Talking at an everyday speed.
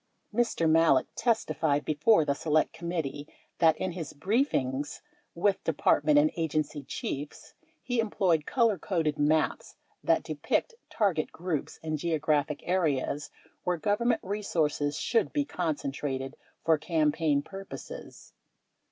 No: slow, 115 wpm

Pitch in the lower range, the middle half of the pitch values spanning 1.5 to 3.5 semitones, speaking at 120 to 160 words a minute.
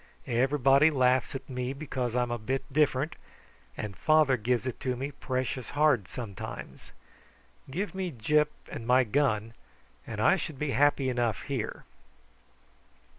Yes: low, 130 Hz; average, 3.2 semitones; average, 140 wpm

